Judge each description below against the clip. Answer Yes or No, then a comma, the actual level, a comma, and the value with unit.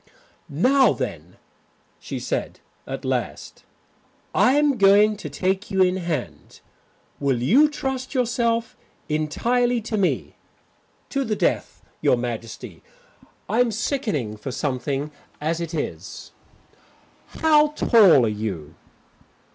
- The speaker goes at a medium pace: No, slow, 115 wpm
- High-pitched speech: Yes, high, 195 Hz